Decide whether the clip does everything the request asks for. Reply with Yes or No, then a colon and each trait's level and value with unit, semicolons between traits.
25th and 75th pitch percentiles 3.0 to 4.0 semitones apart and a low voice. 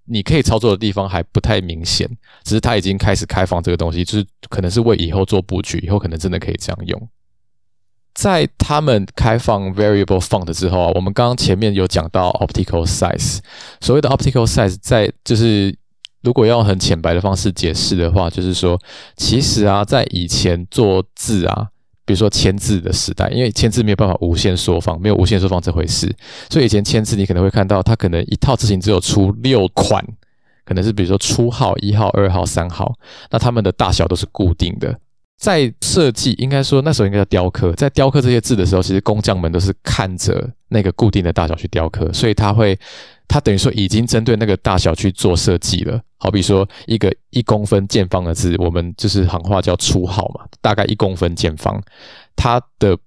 Yes: average, 3.5 semitones; low, 100 Hz